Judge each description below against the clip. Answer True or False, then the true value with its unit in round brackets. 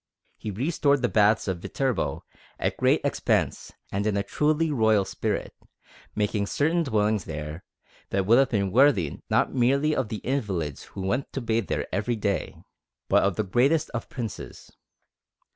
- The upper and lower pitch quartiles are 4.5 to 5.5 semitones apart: True (5.2 semitones)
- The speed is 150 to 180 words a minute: True (160 wpm)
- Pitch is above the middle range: False (110 Hz)